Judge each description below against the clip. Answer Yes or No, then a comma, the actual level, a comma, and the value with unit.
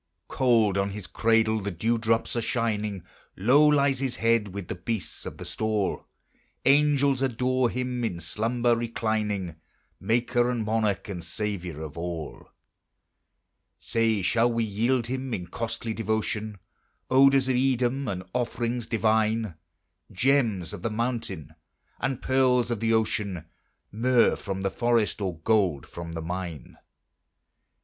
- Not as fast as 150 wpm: Yes, average, 140 wpm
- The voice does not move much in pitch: No, average, 3.6 semitones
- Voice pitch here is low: Yes, low, 115 Hz